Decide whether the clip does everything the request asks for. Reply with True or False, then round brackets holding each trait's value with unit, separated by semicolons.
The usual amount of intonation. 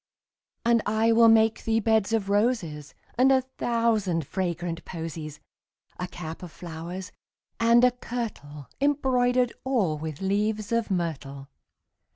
False (5.8 semitones)